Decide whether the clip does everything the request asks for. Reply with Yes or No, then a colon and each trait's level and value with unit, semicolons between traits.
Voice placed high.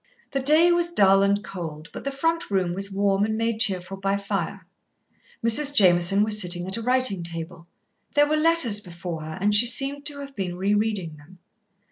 Yes: high, 200 Hz